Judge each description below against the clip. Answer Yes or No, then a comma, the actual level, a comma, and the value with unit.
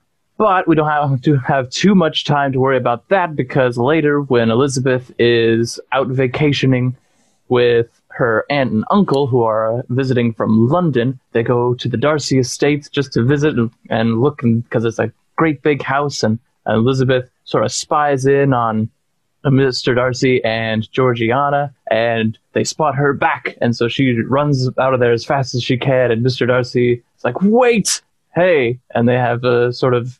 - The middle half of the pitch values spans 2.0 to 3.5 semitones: Yes, average, 3.2 semitones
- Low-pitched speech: Yes, low, 130 Hz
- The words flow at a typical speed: Yes, average, 180 wpm